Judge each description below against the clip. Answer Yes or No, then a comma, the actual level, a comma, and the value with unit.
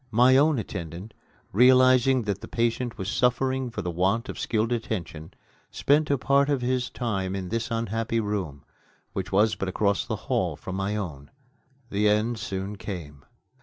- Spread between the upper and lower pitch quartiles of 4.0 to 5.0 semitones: Yes, average, 4.4 semitones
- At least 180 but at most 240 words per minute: No, average, 165 wpm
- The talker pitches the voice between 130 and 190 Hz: No, low, 110 Hz